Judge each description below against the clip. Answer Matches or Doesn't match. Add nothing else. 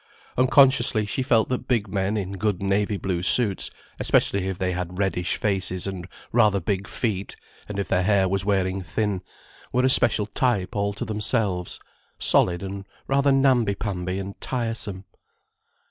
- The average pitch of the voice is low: Matches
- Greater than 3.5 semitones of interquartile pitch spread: Doesn't match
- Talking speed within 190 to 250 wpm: Doesn't match